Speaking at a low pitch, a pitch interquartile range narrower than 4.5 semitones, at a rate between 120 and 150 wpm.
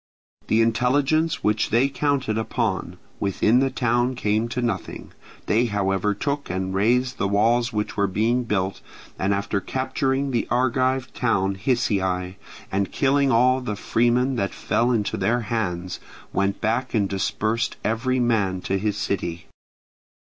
Yes: low, 115 Hz; average, 4.1 semitones; average, 145 wpm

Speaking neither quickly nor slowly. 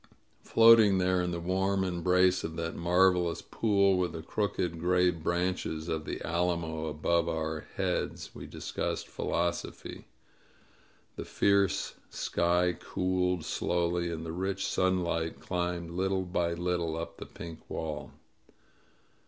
No: slow, 130 wpm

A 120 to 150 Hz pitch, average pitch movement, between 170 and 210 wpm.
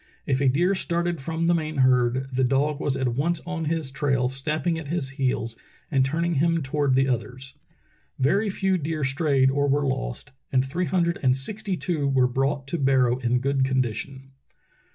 Yes: medium, 140 Hz; average, 3.7 semitones; average, 185 wpm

